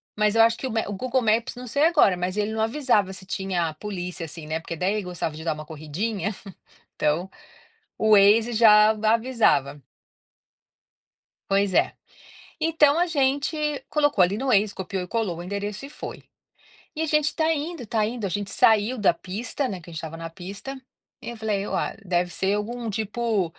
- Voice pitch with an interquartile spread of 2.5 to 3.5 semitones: No, average, 4.8 semitones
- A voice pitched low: No, high, 210 Hz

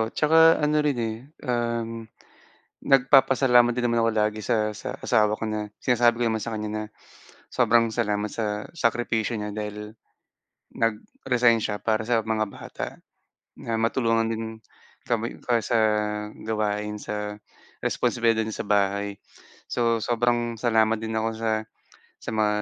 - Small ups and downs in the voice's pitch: Yes, narrow, 1.8 semitones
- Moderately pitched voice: No, low, 115 Hz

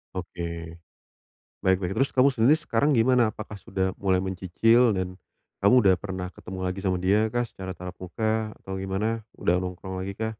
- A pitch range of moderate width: Yes, average, 3.3 semitones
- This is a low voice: Yes, very low, 95 Hz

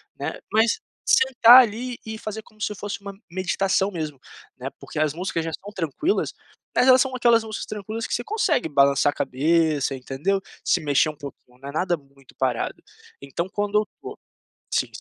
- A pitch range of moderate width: No, wide, 7.1 semitones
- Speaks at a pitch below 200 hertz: Yes, high, 190 Hz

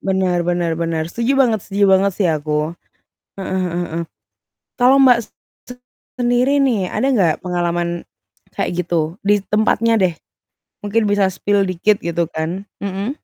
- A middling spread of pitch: Yes, average, 3.9 semitones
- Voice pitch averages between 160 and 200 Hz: Yes, high, 190 Hz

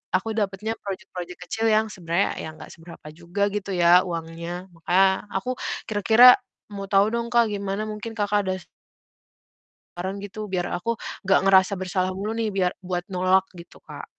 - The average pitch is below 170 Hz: No, high, 195 Hz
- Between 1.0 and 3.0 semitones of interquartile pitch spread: Yes, average, 2.7 semitones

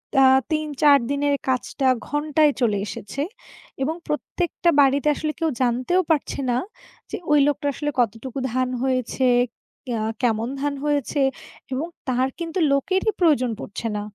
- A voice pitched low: No, very high, 280 Hz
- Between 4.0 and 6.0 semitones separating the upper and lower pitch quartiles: No, average, 3.1 semitones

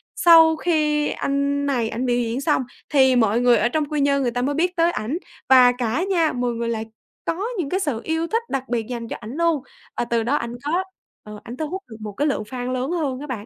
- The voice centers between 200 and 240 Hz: No, very high, 265 Hz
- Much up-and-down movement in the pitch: No, average, 4.6 semitones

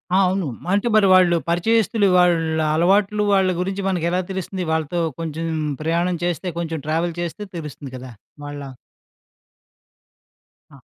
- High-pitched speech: No, medium, 175 Hz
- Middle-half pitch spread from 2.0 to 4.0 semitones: Yes, average, 2.9 semitones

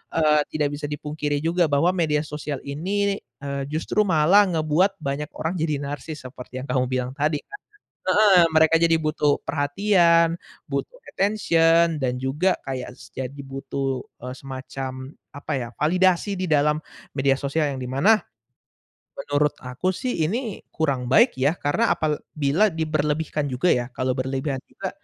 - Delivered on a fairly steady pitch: No, average, 3.6 semitones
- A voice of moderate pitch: Yes, medium, 150 Hz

